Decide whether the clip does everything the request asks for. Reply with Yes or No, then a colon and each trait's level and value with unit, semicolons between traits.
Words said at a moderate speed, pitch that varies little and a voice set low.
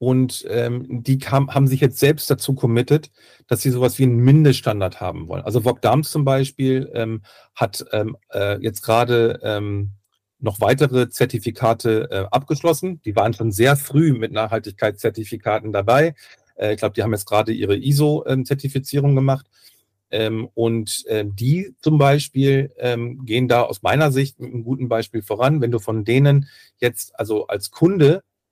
No: average, 165 wpm; average, 3.6 semitones; low, 125 Hz